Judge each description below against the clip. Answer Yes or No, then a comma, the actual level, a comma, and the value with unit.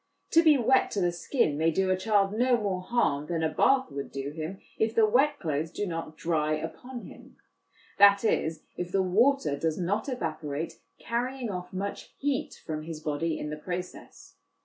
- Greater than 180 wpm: Yes, average, 190 wpm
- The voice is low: No, medium, 185 Hz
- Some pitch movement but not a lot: No, wide, 6.5 semitones